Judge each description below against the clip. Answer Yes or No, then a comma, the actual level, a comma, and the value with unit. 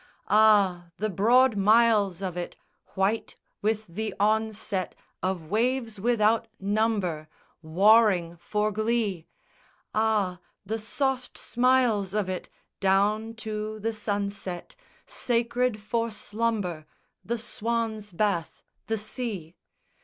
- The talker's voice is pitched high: Yes, high, 215 Hz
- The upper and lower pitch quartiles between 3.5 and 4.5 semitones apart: No, average, 2.7 semitones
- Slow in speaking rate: Yes, slow, 105 wpm